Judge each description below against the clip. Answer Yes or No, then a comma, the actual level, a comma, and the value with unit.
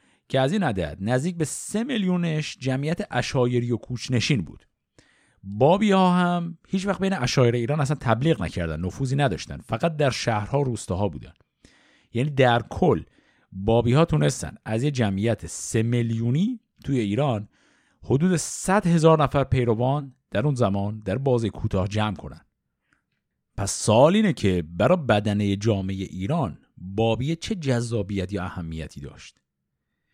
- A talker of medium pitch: No, low, 120 Hz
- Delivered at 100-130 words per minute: No, average, 145 wpm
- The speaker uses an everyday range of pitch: No, wide, 6.7 semitones